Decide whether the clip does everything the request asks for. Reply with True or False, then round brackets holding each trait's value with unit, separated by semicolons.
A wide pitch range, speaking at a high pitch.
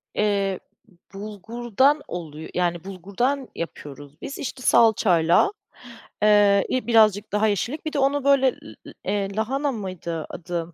True (5.7 semitones; 205 Hz)